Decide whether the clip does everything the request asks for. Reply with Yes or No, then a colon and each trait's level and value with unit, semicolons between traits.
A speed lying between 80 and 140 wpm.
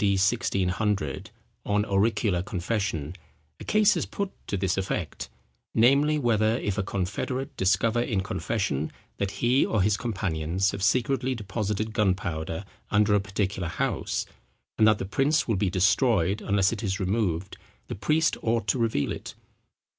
No: average, 150 wpm